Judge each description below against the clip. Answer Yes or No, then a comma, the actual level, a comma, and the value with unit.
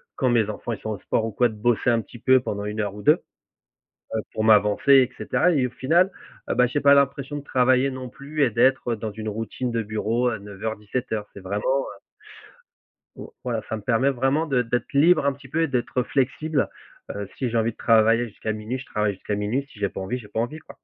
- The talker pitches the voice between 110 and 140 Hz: Yes, low, 120 Hz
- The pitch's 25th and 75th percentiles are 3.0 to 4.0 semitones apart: Yes, average, 3.7 semitones